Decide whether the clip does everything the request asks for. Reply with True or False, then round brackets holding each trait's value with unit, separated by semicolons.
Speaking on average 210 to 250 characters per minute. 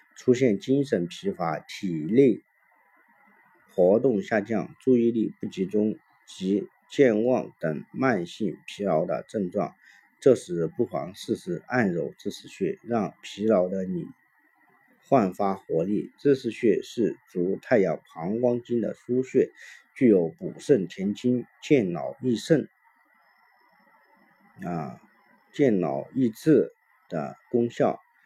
False (170 characters per minute)